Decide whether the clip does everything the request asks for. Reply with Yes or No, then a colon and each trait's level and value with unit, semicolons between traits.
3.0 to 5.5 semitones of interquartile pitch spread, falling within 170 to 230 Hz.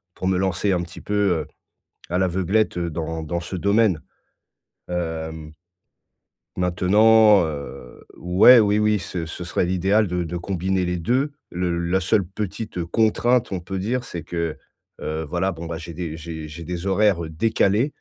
No: average, 3.4 semitones; very low, 90 Hz